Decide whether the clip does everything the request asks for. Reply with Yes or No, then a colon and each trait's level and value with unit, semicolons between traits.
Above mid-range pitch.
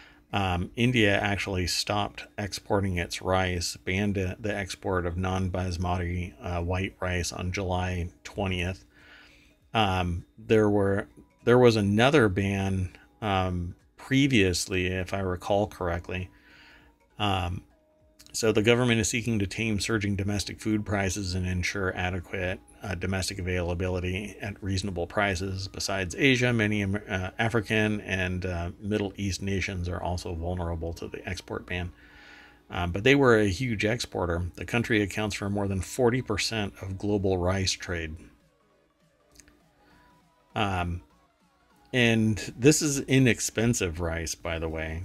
No: very low, 95 Hz